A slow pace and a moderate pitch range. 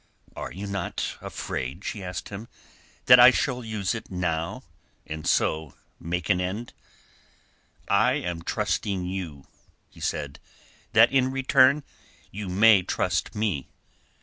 Yes: slow, 130 wpm; average, 4.9 semitones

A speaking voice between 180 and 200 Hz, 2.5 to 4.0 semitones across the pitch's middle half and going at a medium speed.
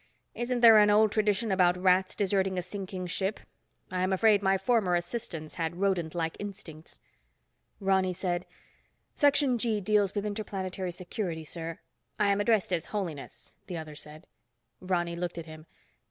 Yes: high, 190 Hz; average, 3.0 semitones; average, 155 wpm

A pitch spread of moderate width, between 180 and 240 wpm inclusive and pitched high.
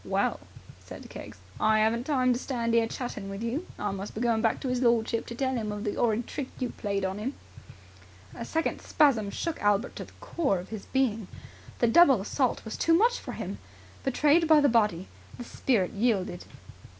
Yes: average, 4.2 semitones; average, 200 wpm; high, 235 Hz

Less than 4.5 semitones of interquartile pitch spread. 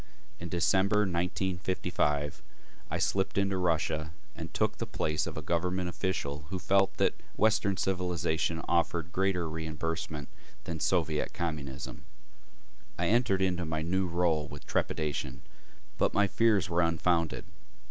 Yes: average, 3.1 semitones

